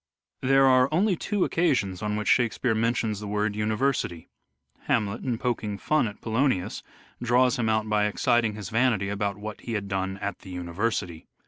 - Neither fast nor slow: Yes, average, 185 wpm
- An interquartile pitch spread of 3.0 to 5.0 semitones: Yes, average, 3.5 semitones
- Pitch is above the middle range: No, low, 110 Hz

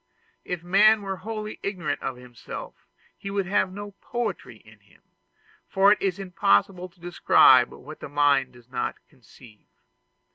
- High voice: No, medium, 180 Hz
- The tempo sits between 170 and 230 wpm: No, average, 150 wpm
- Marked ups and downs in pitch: Yes, wide, 7.1 semitones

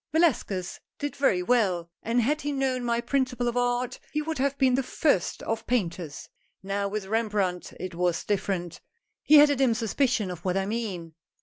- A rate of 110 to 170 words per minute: No, average, 190 wpm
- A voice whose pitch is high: Yes, high, 230 Hz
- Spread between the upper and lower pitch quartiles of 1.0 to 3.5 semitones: No, wide, 5.5 semitones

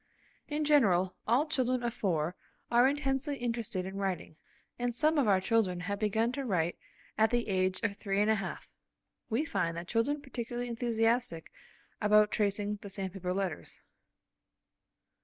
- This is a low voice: No, high, 220 Hz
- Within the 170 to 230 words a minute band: No, average, 155 wpm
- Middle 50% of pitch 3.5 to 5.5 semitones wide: Yes, average, 4.3 semitones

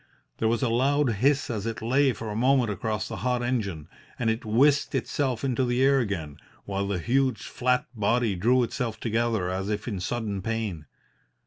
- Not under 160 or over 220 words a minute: Yes, average, 190 wpm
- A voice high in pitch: No, low, 115 Hz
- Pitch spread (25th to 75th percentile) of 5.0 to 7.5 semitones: No, average, 3.5 semitones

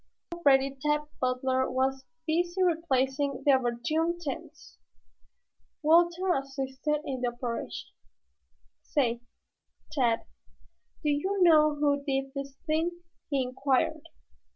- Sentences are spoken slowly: Yes, slow, 105 wpm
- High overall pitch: Yes, very high, 280 Hz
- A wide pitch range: No, average, 3.3 semitones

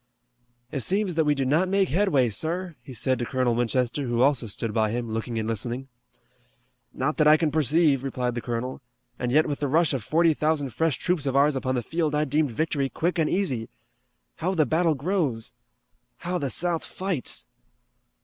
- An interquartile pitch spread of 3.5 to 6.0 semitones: Yes, average, 4.5 semitones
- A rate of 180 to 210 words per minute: Yes, average, 195 wpm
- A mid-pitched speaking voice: Yes, medium, 145 Hz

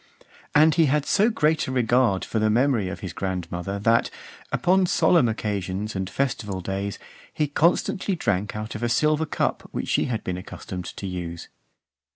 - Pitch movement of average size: No, wide, 7.5 semitones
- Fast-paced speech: No, average, 175 wpm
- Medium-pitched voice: No, low, 110 Hz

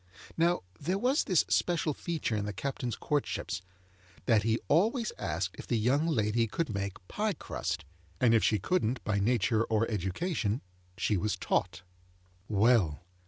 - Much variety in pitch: Yes, wide, 7.7 semitones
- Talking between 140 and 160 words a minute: Yes, average, 155 wpm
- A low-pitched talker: Yes, low, 115 Hz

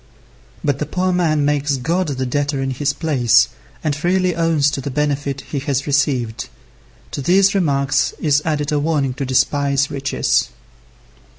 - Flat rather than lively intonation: Yes, narrow, 2.1 semitones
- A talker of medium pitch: Yes, medium, 145 Hz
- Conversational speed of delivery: Yes, average, 160 wpm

